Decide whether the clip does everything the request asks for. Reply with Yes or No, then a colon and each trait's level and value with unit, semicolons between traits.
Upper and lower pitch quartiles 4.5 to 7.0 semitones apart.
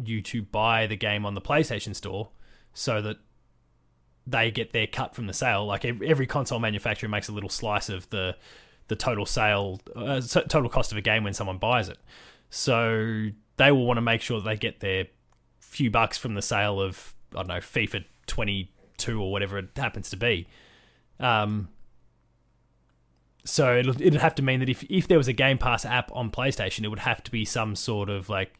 No: average, 3.5 semitones